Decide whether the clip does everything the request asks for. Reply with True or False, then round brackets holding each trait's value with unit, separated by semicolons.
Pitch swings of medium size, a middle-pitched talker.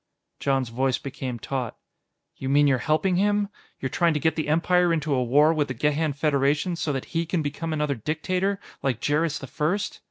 True (3.5 semitones; 150 Hz)